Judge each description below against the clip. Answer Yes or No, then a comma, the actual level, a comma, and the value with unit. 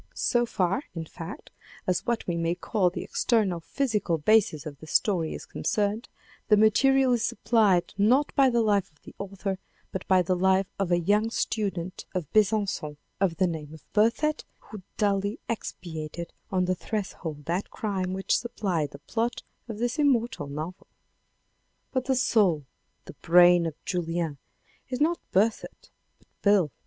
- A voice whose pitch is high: Yes, high, 195 Hz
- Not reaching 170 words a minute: Yes, average, 160 wpm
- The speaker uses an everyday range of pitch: Yes, average, 4.6 semitones